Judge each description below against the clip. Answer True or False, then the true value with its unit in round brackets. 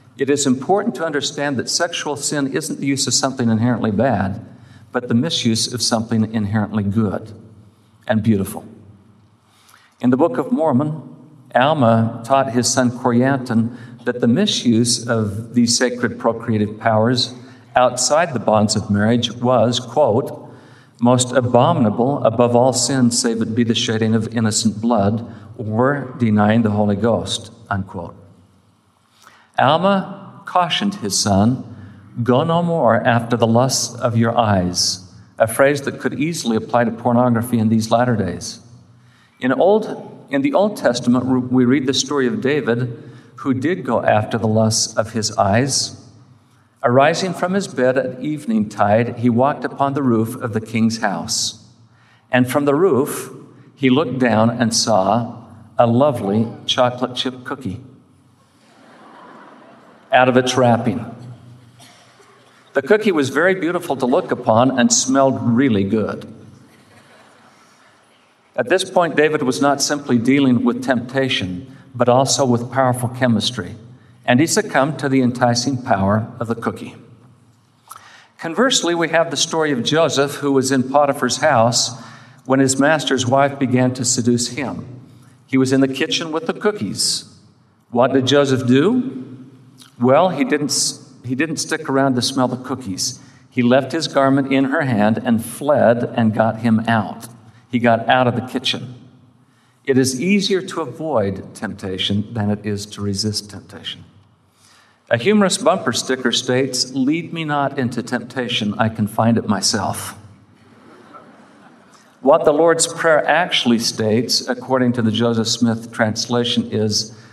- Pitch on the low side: True (125 Hz)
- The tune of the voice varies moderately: True (3.0 semitones)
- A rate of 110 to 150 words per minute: True (145 wpm)